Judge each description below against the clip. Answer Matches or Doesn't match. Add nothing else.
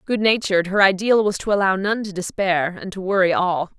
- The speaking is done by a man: Doesn't match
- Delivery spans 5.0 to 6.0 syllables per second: Matches